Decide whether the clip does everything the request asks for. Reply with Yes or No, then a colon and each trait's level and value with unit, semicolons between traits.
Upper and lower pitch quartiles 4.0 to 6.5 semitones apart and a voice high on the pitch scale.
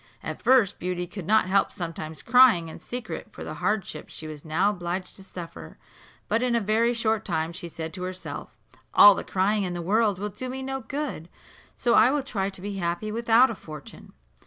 Yes: average, 4.9 semitones; high, 195 Hz